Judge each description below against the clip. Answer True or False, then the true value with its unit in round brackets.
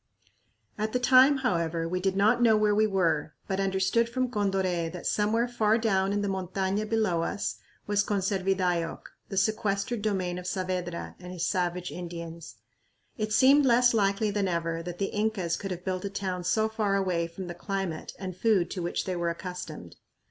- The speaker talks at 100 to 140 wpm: False (185 wpm)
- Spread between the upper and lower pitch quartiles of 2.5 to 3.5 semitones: True (3.1 semitones)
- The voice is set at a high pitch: True (195 Hz)